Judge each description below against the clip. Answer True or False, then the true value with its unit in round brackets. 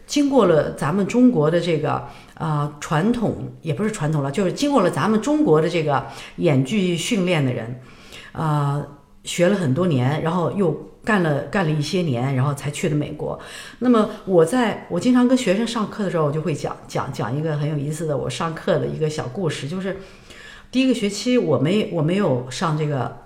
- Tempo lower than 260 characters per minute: False (290 characters per minute)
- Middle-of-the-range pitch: True (165 Hz)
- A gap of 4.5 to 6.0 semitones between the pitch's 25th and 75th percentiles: True (5.5 semitones)